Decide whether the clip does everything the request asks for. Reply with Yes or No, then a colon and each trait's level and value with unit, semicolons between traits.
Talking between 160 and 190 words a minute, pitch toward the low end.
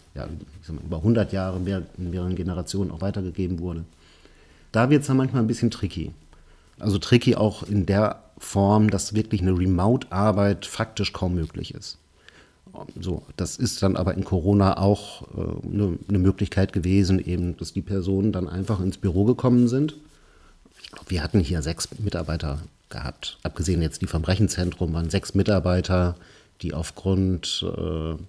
Yes: average, 165 wpm; very low, 95 Hz